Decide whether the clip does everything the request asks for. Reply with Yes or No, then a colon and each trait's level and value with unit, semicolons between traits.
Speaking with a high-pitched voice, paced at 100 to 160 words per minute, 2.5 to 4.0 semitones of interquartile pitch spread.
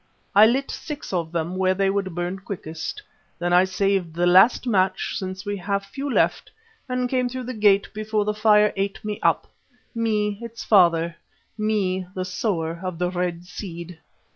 No: high, 195 Hz; average, 175 wpm; average, 3.2 semitones